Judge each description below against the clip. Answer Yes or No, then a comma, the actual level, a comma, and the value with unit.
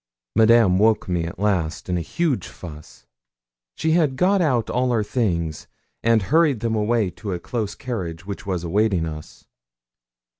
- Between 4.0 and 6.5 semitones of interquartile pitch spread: Yes, wide, 5.4 semitones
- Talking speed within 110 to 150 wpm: No, average, 160 wpm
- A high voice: No, low, 105 Hz